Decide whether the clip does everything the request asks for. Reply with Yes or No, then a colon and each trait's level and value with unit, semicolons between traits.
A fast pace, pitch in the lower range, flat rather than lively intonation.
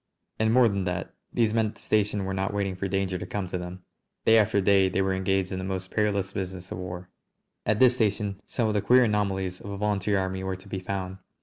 Yes: fast, 250 wpm; very low, 95 Hz; narrow, 1.8 semitones